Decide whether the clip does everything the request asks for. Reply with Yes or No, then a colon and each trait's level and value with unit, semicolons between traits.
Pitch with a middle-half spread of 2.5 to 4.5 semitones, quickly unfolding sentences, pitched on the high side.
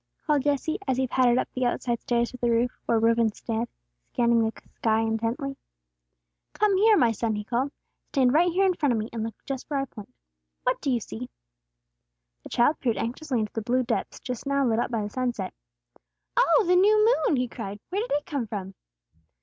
Yes: average, 4.1 semitones; fast, 210 wpm; high, 245 Hz